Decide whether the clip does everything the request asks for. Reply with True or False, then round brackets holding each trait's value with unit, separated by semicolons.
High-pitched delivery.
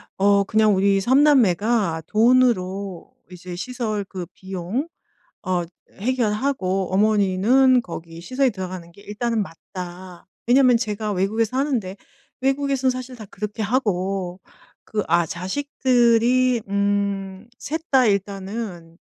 True (205 Hz)